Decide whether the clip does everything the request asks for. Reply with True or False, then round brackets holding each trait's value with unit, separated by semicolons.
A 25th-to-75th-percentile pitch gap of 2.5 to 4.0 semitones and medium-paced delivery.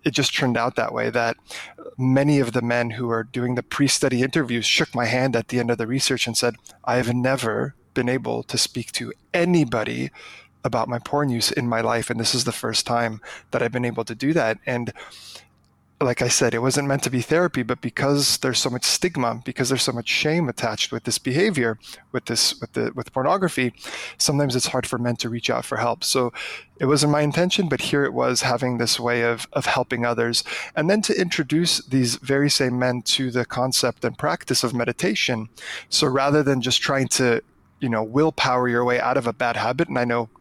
False (2.9 semitones; 220 wpm)